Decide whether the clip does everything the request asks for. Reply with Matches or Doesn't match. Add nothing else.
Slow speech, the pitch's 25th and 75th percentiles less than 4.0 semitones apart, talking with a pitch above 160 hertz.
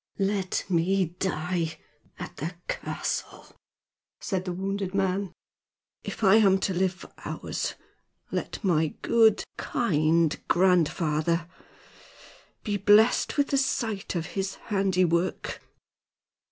Matches